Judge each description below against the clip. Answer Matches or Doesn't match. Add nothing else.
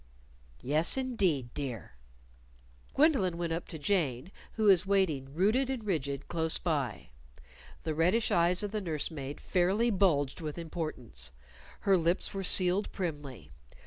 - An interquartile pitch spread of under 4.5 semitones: Doesn't match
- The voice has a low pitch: Doesn't match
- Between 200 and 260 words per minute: Doesn't match